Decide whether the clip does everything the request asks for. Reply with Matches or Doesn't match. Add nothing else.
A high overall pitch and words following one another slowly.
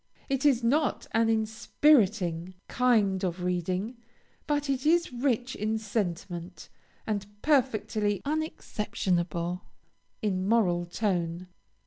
Matches